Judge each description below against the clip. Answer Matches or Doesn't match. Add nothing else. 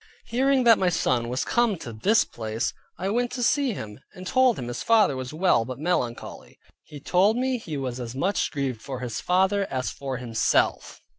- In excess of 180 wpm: Matches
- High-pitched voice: Doesn't match